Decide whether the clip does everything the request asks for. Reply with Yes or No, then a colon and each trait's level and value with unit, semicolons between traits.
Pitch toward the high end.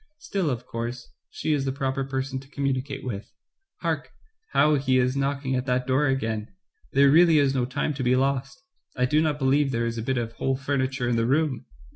No: low, 135 Hz